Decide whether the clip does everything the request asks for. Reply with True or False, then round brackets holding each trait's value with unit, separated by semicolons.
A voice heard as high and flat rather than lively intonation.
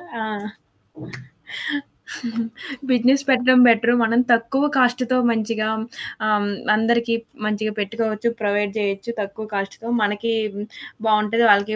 True (225 Hz; 2.2 semitones)